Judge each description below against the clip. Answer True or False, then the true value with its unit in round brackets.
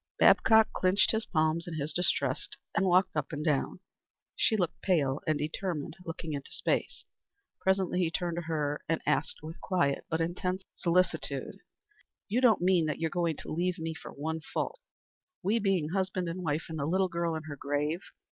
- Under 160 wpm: False (185 wpm)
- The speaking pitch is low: False (170 Hz)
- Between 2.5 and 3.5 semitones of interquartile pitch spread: True (2.9 semitones)